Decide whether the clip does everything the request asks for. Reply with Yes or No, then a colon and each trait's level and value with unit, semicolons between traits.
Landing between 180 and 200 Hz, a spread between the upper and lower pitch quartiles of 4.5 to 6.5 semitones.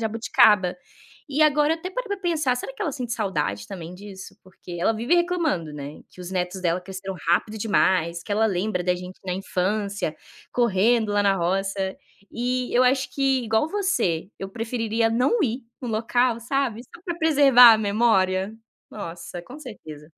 No: high, 220 Hz; average, 5.2 semitones